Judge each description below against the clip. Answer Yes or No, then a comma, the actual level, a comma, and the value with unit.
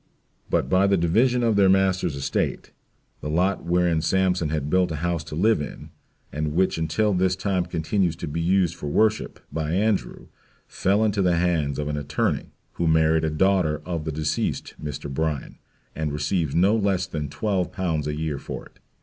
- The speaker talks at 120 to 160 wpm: No, average, 185 wpm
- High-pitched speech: No, very low, 85 Hz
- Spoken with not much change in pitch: No, average, 3.6 semitones